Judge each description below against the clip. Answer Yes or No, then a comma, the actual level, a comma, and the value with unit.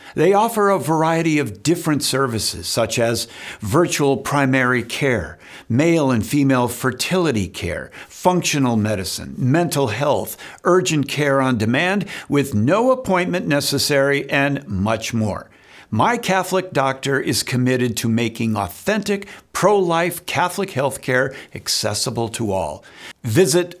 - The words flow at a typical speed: No, slow, 125 wpm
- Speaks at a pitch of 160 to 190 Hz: No, low, 135 Hz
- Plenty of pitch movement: Yes, wide, 6.7 semitones